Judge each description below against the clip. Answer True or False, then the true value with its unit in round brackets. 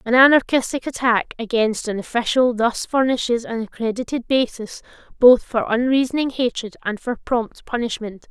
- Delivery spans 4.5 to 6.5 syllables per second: True (5.0 syllables/s)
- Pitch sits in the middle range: False (240 Hz)